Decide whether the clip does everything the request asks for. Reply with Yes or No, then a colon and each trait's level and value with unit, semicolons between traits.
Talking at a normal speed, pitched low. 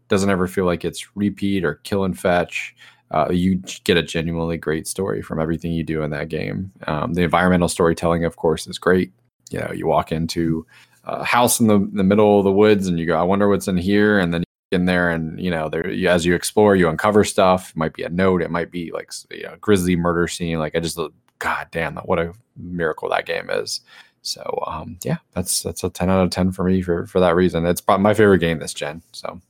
No: fast, 245 wpm; very low, 90 Hz